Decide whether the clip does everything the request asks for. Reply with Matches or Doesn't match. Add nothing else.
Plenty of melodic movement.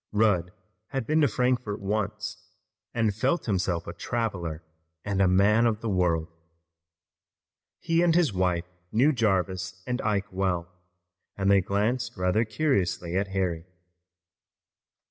Doesn't match